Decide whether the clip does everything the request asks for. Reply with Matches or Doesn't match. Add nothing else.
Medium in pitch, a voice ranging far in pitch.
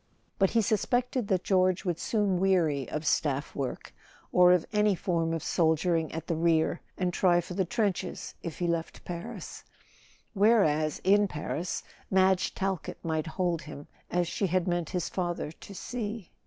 Doesn't match